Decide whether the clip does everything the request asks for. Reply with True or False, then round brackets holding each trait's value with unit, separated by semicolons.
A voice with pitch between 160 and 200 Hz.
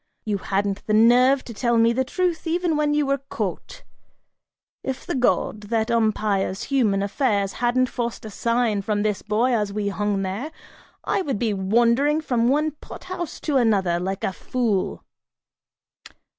False (230 Hz)